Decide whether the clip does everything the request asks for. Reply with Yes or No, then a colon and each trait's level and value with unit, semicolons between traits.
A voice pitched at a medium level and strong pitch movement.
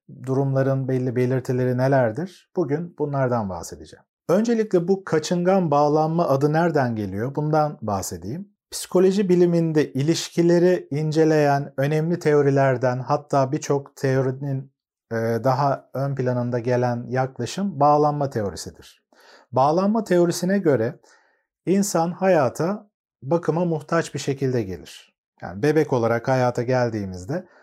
No: medium, 145 Hz; average, 4.7 semitones